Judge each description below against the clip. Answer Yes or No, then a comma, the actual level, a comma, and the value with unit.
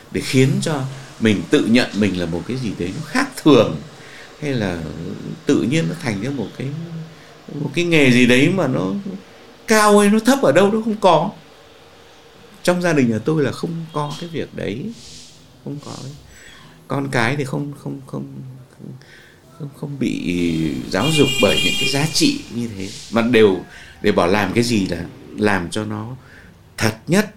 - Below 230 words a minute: Yes, average, 185 wpm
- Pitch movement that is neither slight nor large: No, wide, 6.9 semitones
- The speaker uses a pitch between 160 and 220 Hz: No, low, 135 Hz